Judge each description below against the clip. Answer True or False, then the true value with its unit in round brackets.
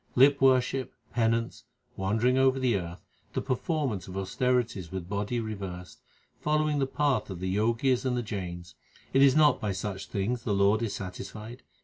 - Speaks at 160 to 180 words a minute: True (170 wpm)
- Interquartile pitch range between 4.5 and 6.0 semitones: True (5.1 semitones)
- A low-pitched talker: True (115 Hz)